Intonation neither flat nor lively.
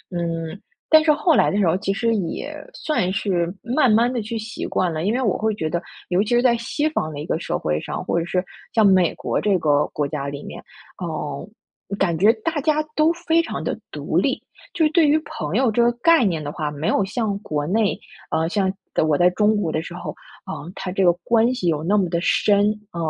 No: wide, 6.0 semitones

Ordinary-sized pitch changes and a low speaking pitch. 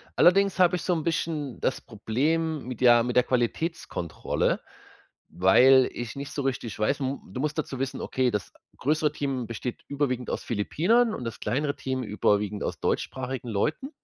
Yes: average, 4.3 semitones; low, 130 Hz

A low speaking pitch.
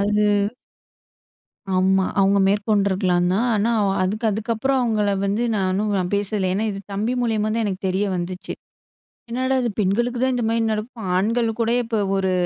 No: high, 210 Hz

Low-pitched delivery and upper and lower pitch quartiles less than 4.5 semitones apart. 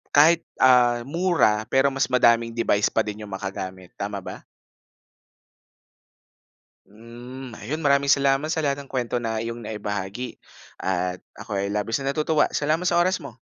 No: low, 120 Hz; average, 4.8 semitones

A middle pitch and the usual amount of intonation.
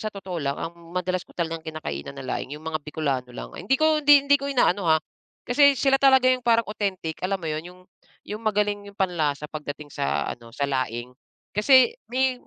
No: medium, 180 Hz; wide, 8.6 semitones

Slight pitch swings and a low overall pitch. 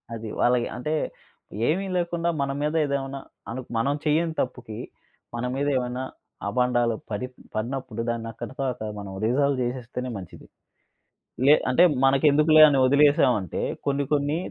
No: average, 3.2 semitones; low, 130 Hz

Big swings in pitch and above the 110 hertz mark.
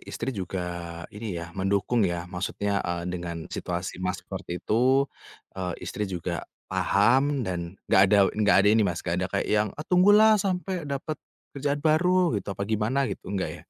No: wide, 7.4 semitones; low, 100 Hz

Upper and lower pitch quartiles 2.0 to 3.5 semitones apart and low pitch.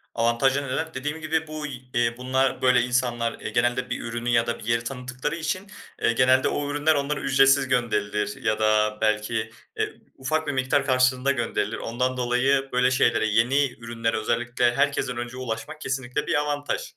Yes: average, 2.8 semitones; low, 125 Hz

